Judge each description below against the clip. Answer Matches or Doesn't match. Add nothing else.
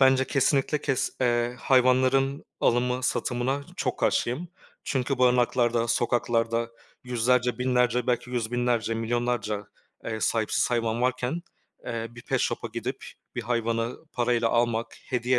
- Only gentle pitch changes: Matches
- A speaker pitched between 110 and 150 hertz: Matches